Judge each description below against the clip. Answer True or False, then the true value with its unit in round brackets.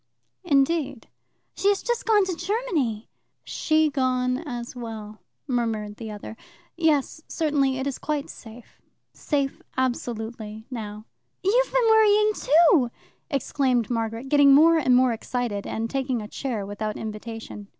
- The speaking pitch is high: True (255 Hz)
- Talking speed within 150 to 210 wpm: False (135 wpm)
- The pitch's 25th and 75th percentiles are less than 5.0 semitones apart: False (5.6 semitones)